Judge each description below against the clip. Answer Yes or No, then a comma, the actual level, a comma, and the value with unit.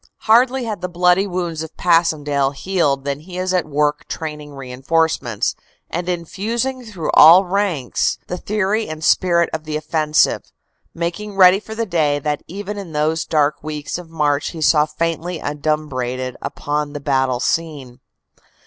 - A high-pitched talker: No, medium, 160 Hz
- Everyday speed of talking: Yes, average, 155 wpm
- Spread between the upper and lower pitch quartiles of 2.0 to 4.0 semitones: Yes, average, 3.7 semitones